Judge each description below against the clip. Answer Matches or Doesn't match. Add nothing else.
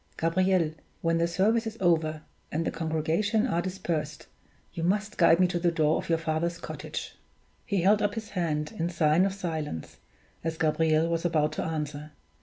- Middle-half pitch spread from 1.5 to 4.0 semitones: Matches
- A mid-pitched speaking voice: Matches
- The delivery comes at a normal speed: Matches